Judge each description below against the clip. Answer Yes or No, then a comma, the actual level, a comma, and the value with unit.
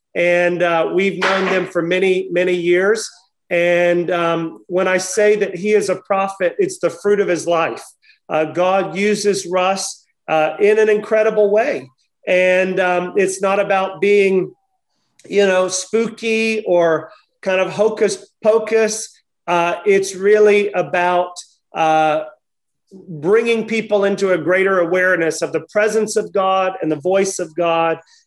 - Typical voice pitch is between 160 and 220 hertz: Yes, high, 190 Hz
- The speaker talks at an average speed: Yes, average, 145 wpm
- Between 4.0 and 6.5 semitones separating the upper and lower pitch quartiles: No, average, 2.8 semitones